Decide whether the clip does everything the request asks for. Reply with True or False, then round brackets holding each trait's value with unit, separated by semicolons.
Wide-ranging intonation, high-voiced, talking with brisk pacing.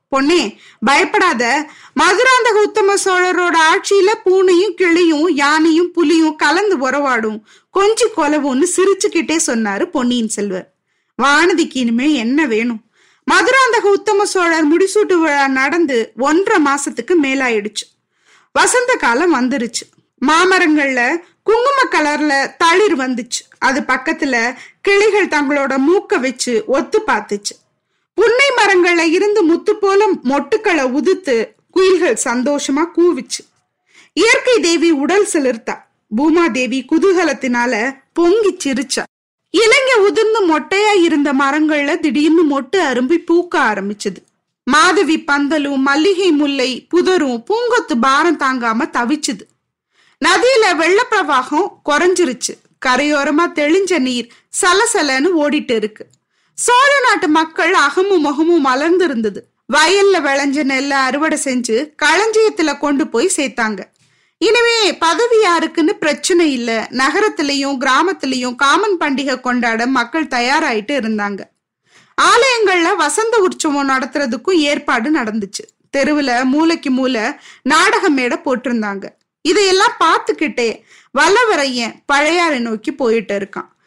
False (5.9 semitones; 315 Hz; 100 wpm)